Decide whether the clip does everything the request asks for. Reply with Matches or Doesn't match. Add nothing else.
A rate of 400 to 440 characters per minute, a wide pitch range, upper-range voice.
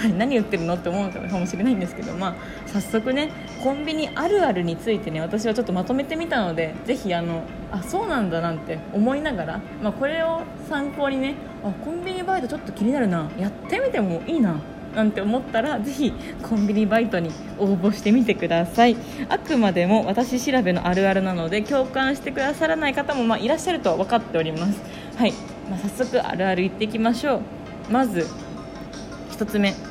Matches